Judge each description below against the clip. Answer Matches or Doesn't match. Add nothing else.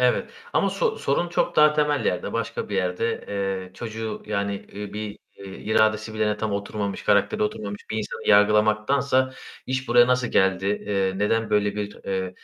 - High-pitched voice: Doesn't match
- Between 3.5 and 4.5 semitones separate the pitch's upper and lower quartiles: Doesn't match